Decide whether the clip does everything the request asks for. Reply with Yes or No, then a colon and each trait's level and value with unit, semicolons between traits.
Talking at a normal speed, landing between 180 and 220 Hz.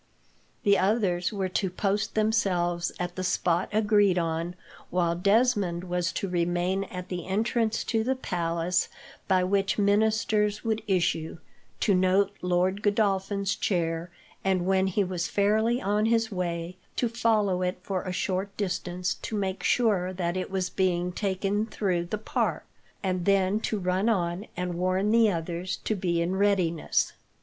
Yes: average, 155 wpm; high, 190 Hz